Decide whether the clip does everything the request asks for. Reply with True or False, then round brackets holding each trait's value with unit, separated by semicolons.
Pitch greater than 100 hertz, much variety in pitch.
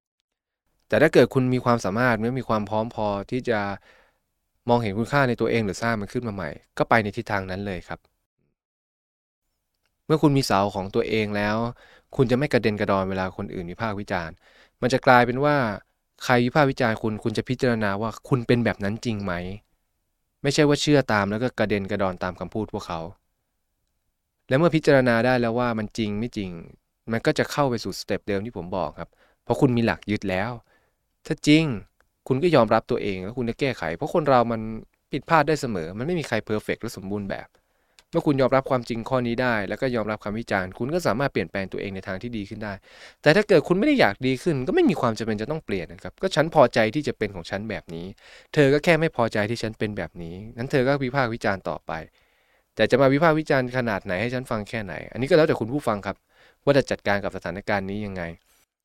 False (115 Hz; 4.1 semitones)